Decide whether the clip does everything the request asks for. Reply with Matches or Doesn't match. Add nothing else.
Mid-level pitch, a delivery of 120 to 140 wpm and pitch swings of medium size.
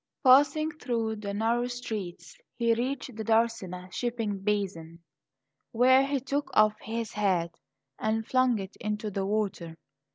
Doesn't match